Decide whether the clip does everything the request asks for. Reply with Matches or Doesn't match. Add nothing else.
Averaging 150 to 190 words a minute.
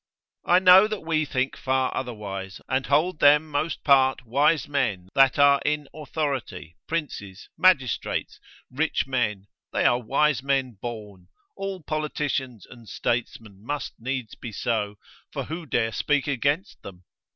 Doesn't match